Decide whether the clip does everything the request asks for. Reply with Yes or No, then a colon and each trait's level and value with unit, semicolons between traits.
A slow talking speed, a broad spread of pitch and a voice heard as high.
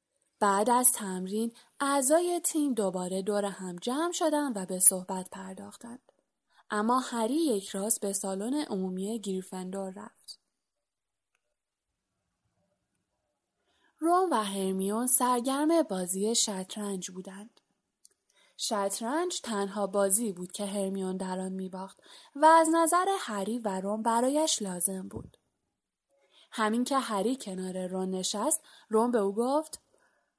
No: average, 115 wpm; wide, 5.8 semitones; high, 210 Hz